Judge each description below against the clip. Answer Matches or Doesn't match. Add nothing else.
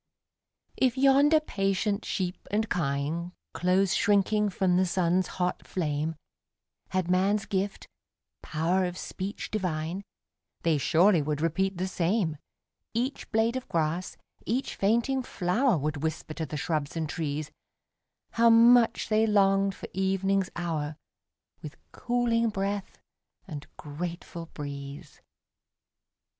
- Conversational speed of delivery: Doesn't match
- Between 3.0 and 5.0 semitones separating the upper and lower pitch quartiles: Matches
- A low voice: Doesn't match